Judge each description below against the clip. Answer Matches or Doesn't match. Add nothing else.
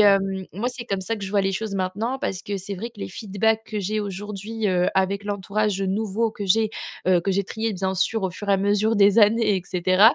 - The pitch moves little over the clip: Matches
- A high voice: Matches